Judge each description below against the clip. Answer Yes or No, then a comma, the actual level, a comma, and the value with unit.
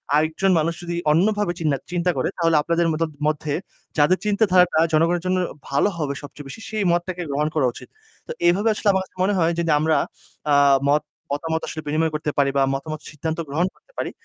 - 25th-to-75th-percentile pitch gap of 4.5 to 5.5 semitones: No, average, 3.0 semitones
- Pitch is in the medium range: Yes, medium, 165 Hz